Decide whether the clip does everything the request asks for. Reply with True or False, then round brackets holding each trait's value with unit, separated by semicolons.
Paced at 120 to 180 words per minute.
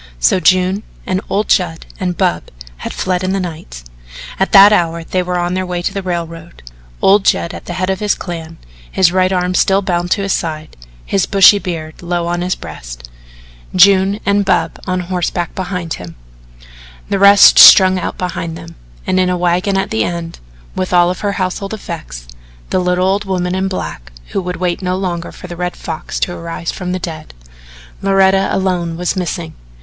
False (190 wpm)